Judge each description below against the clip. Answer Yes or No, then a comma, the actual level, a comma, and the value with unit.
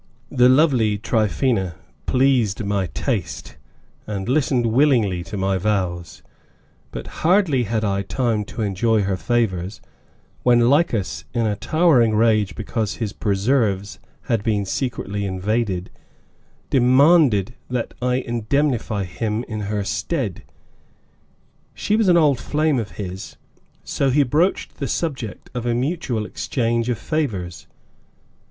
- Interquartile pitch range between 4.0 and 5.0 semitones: Yes, average, 4.3 semitones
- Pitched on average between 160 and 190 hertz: No, low, 115 Hz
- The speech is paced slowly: Yes, slow, 130 wpm